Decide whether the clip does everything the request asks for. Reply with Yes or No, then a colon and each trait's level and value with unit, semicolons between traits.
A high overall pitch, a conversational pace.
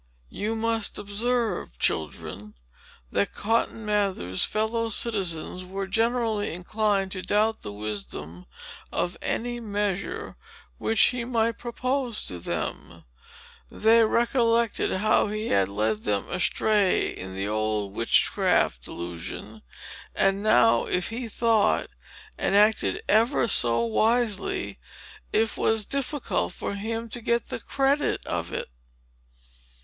No: high, 210 Hz; slow, 120 wpm